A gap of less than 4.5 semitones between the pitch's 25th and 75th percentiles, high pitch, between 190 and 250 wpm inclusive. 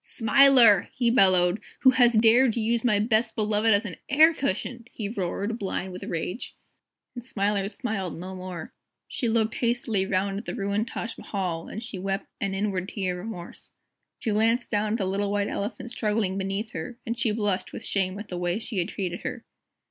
Yes: average, 3.3 semitones; high, 210 Hz; average, 195 wpm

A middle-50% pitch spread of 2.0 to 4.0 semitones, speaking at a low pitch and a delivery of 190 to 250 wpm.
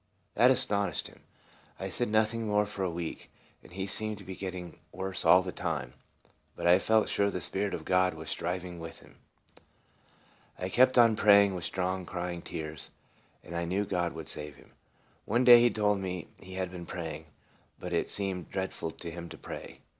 Yes: average, 2.9 semitones; very low, 95 Hz; average, 200 wpm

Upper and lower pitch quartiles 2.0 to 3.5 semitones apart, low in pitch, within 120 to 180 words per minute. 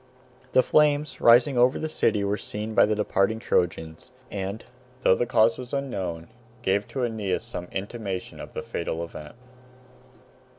No: average, 4.3 semitones; low, 105 Hz; average, 155 wpm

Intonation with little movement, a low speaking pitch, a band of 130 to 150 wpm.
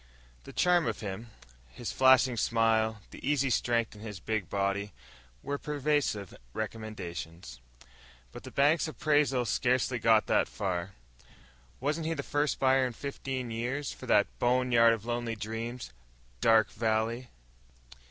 No: average, 3.5 semitones; low, 115 Hz; average, 140 wpm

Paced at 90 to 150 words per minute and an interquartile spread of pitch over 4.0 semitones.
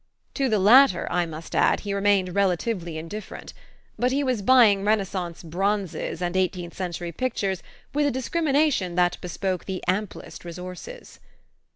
Yes: average, 145 wpm; average, 4.6 semitones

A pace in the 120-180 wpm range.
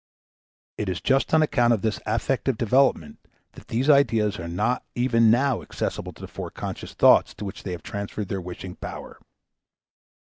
Yes: average, 170 wpm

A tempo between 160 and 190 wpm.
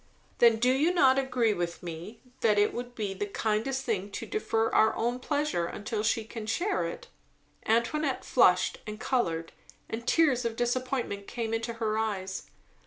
Yes: average, 170 wpm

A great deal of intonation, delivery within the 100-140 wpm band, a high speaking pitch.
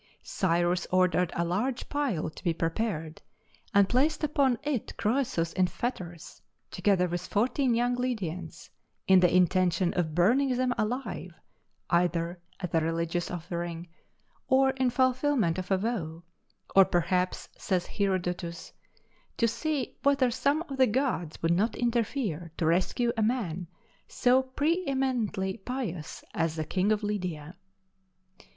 Yes: wide, 6.4 semitones; slow, 135 wpm; high, 195 Hz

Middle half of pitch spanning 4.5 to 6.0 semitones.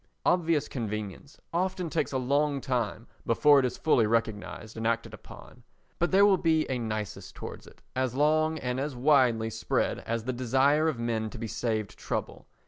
Yes: average, 5.0 semitones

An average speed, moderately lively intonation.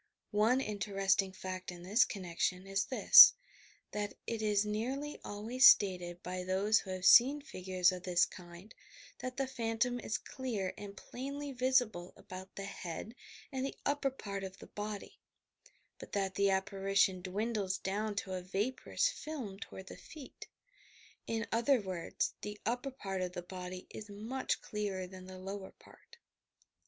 Yes: average, 155 wpm; average, 4.2 semitones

